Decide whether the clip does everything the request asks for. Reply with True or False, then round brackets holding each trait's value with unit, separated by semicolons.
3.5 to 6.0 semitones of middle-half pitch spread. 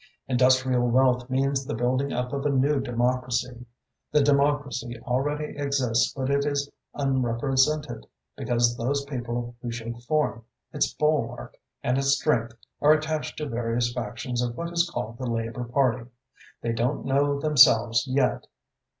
False (2.8 semitones)